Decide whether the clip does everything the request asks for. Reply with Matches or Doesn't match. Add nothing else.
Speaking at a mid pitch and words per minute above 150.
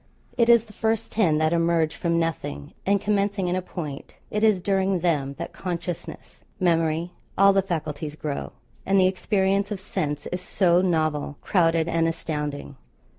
Matches